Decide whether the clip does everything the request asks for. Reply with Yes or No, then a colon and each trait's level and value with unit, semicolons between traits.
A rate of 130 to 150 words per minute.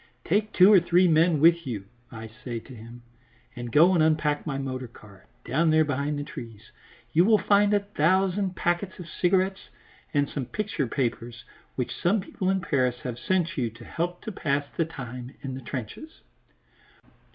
No: average, 180 wpm